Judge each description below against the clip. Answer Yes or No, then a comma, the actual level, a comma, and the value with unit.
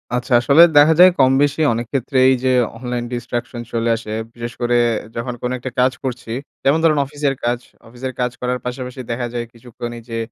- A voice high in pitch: No, low, 125 Hz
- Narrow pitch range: Yes, narrow, 1.9 semitones